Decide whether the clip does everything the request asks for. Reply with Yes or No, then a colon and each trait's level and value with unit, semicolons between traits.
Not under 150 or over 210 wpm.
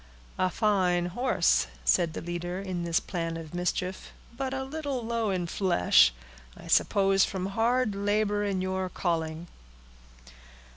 No: average, 140 wpm